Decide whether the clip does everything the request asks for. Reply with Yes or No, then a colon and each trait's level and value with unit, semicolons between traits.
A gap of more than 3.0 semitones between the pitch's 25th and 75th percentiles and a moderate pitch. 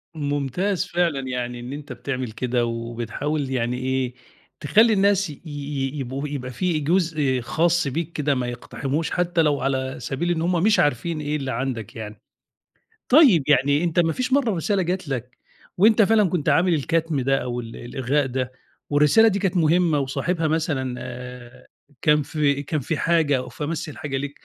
Yes: average, 4.6 semitones; medium, 145 Hz